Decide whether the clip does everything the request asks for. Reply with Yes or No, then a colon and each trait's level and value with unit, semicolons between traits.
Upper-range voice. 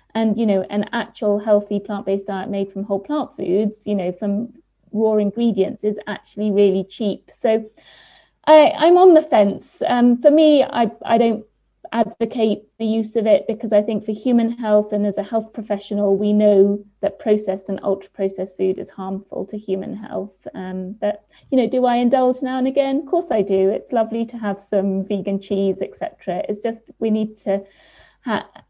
Yes: high, 210 Hz